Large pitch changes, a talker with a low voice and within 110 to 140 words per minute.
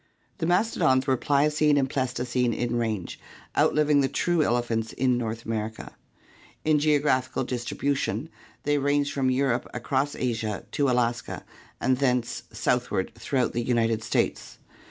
No: average, 3.2 semitones; low, 130 Hz; slow, 135 wpm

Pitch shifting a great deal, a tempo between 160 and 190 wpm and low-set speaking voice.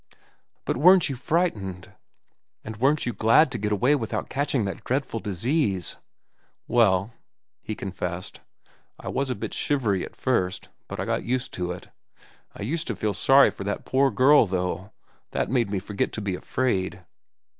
Yes: wide, 5.7 semitones; average, 165 wpm; low, 110 Hz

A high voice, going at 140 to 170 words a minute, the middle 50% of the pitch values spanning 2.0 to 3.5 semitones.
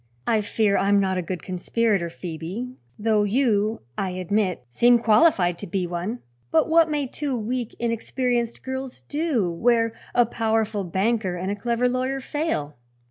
No: high, 220 Hz; average, 160 wpm; average, 4.6 semitones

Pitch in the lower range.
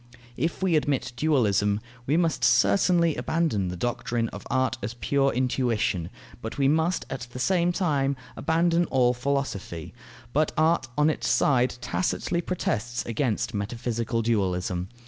Yes: low, 125 Hz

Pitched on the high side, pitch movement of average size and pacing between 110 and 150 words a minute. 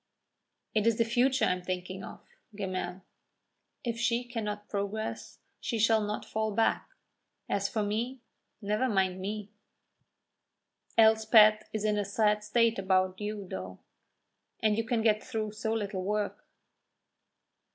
No: high, 210 Hz; narrow, 2.0 semitones; average, 140 wpm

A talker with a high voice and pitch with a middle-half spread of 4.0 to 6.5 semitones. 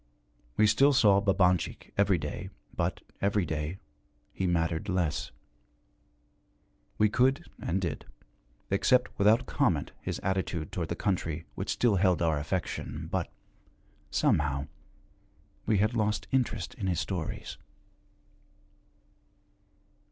No: very low, 95 Hz; average, 4.3 semitones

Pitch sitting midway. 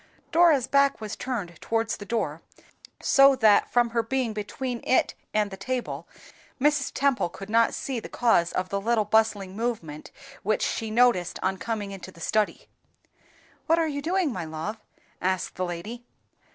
No: high, 225 Hz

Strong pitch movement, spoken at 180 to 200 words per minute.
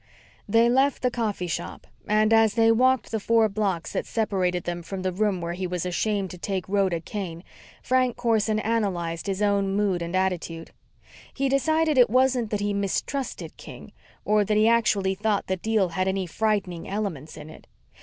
No: average, 3.6 semitones; average, 185 wpm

